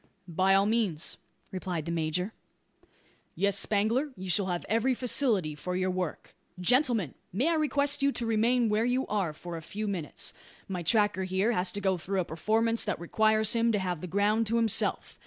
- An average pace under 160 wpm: No, average, 190 wpm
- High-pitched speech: Yes, high, 200 Hz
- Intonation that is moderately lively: Yes, average, 4.0 semitones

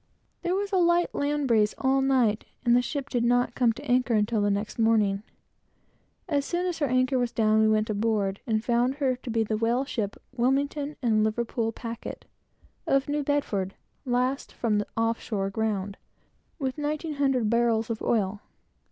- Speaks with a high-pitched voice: Yes, high, 240 Hz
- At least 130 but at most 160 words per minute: No, average, 180 wpm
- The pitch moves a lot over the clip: No, average, 3.9 semitones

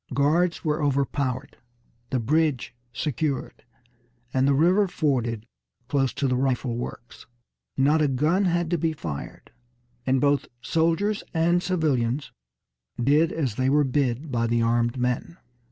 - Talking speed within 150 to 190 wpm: No, slow, 135 wpm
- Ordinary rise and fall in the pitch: Yes, average, 4.3 semitones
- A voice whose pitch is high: No, medium, 140 Hz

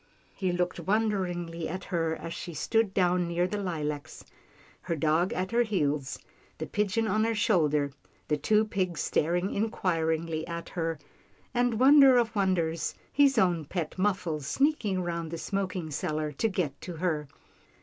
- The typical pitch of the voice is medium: Yes, medium, 180 Hz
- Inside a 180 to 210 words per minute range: No, average, 160 wpm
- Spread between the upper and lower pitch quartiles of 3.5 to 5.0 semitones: Yes, average, 4.3 semitones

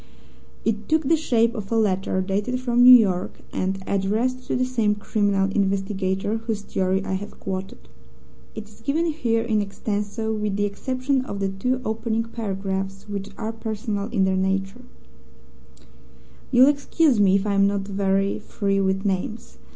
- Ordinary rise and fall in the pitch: Yes, average, 3.0 semitones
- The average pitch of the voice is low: No, high, 205 Hz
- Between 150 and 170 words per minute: Yes, average, 160 wpm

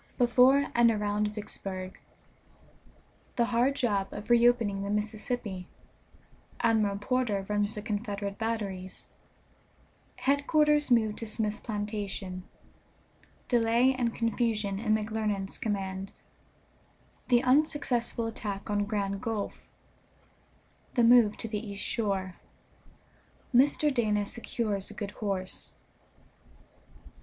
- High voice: Yes, high, 215 Hz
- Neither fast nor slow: No, slow, 100 wpm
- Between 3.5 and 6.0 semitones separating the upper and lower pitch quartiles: No, average, 2.9 semitones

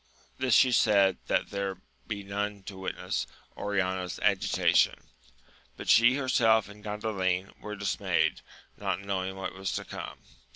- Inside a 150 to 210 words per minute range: No, average, 140 wpm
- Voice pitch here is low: Yes, low, 100 Hz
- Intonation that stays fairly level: Yes, narrow, 1.9 semitones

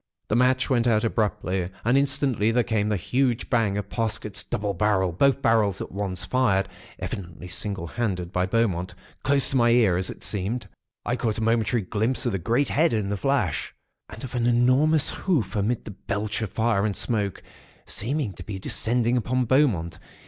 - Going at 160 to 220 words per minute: Yes, average, 185 wpm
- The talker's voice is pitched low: Yes, low, 110 Hz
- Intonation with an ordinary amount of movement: Yes, average, 4.0 semitones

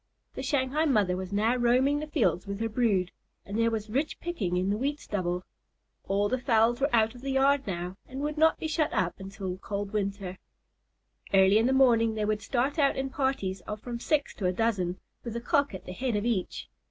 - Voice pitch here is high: Yes, high, 225 Hz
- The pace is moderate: No, fast, 220 wpm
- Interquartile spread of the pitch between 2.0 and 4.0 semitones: No, average, 5.2 semitones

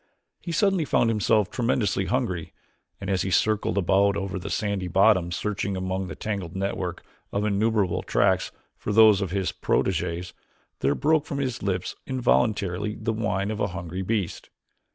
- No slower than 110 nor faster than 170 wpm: Yes, average, 160 wpm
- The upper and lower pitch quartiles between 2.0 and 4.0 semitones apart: Yes, average, 3.0 semitones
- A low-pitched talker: Yes, low, 100 Hz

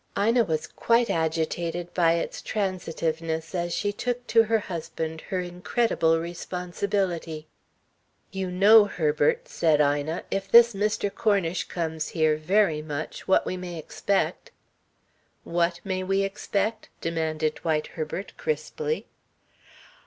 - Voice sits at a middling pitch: Yes, medium, 175 Hz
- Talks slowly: Yes, slow, 125 wpm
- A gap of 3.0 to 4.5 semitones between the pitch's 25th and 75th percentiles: Yes, average, 3.9 semitones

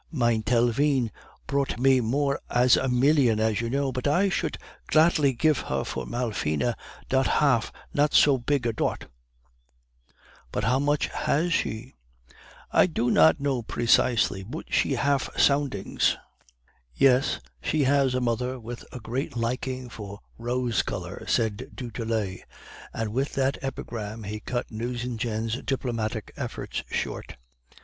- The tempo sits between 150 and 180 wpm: No, average, 140 wpm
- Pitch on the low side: Yes, low, 125 Hz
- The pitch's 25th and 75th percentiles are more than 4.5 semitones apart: No, average, 3.3 semitones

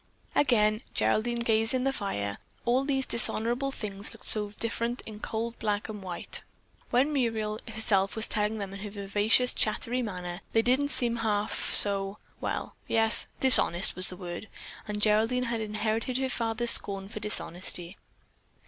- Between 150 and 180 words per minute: Yes, average, 155 wpm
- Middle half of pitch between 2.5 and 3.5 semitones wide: Yes, average, 2.8 semitones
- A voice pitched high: Yes, high, 220 Hz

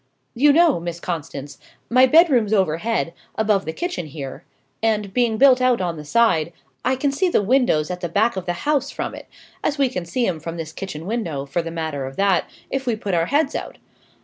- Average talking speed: No, fast, 215 wpm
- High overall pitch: Yes, high, 200 Hz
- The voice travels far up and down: Yes, wide, 7.3 semitones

